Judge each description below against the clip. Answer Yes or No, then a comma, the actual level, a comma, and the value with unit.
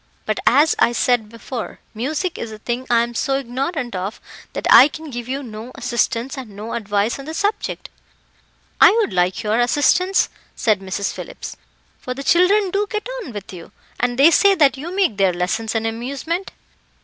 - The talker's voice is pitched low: No, high, 245 Hz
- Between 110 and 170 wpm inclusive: No, average, 185 wpm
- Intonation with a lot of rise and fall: Yes, wide, 5.7 semitones